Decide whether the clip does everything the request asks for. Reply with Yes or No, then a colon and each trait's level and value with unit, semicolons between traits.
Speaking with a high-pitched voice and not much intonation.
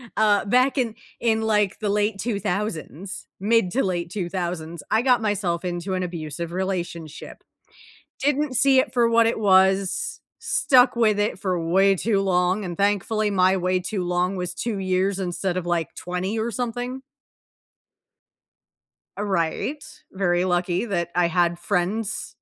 No: high, 195 Hz; average, 3.6 semitones